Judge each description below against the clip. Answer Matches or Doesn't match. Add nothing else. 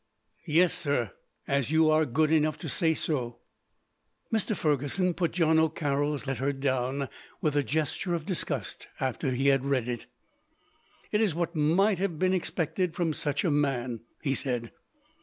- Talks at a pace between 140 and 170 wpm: Matches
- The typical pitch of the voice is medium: Matches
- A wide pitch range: Doesn't match